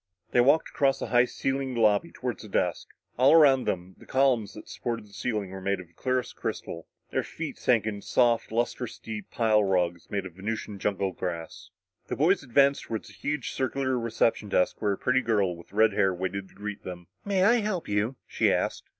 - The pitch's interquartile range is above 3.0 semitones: Yes, average, 5.0 semitones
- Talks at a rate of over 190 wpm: Yes, fast, 205 wpm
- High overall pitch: No, low, 110 Hz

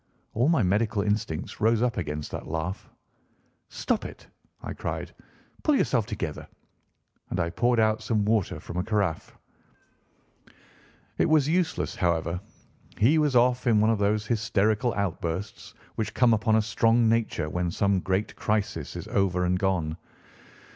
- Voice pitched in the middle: No, low, 105 Hz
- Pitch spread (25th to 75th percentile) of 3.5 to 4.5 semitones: Yes, average, 4.0 semitones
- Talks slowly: No, average, 150 wpm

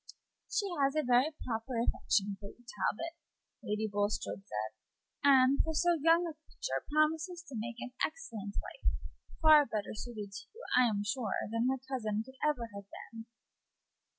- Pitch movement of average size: No, wide, 6.3 semitones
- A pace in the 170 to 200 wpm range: No, average, 160 wpm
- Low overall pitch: No, high, 245 Hz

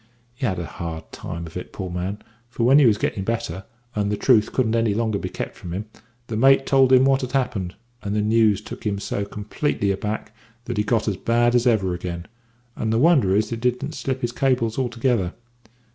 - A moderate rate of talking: No, fast, 220 wpm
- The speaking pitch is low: Yes, low, 110 Hz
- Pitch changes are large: No, average, 3.9 semitones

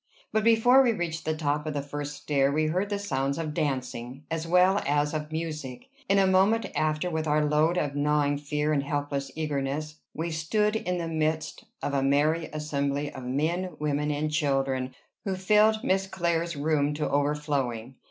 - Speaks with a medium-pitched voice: Yes, medium, 150 Hz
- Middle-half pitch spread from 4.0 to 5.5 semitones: No, average, 3.0 semitones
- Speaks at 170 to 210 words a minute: Yes, average, 180 wpm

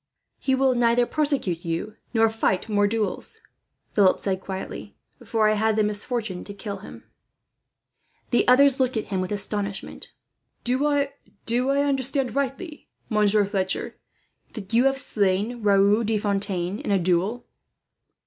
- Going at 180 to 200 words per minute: No, average, 140 wpm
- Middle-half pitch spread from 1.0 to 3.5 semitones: No, average, 4.0 semitones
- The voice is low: No, high, 215 Hz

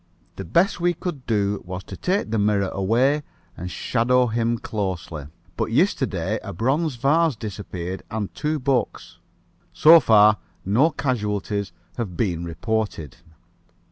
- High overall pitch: No, low, 110 Hz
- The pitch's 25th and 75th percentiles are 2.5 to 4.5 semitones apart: No, wide, 5.4 semitones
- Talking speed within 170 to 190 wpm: No, slow, 135 wpm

